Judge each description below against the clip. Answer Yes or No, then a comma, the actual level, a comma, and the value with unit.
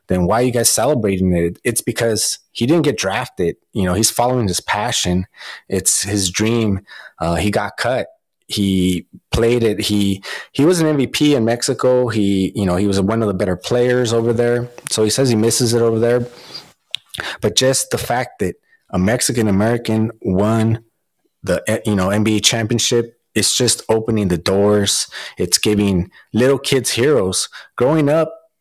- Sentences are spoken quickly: No, average, 170 wpm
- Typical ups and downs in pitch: Yes, average, 3.2 semitones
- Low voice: Yes, low, 110 Hz